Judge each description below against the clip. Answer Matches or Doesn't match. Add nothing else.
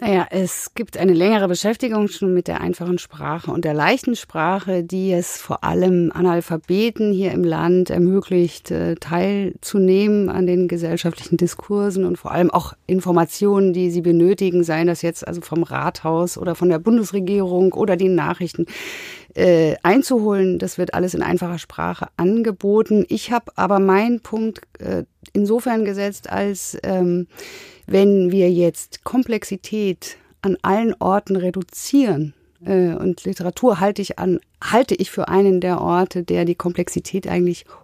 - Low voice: Doesn't match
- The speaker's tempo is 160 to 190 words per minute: Doesn't match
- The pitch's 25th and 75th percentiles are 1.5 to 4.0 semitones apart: Matches